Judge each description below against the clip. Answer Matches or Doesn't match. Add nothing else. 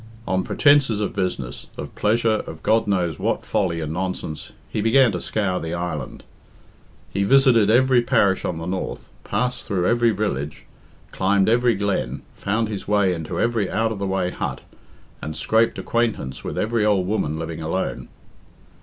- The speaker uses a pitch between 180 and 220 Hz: Doesn't match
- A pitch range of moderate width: Matches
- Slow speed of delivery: Doesn't match